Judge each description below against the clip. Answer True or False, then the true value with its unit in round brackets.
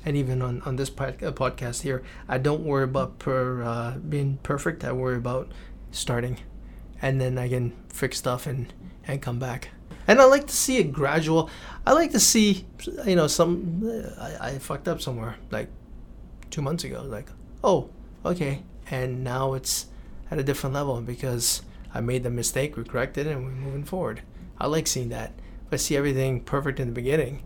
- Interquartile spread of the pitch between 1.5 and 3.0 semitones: False (3.4 semitones)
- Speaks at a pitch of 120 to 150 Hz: True (135 Hz)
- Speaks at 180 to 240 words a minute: True (190 wpm)